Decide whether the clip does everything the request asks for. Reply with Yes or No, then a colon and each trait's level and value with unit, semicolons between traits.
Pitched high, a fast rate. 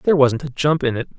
No: medium, 140 Hz; fast, 305 wpm